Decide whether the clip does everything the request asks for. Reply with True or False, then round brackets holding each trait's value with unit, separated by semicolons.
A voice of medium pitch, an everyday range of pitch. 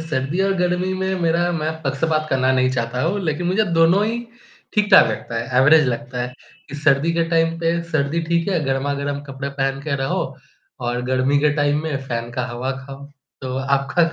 True (145 Hz; 4.1 semitones)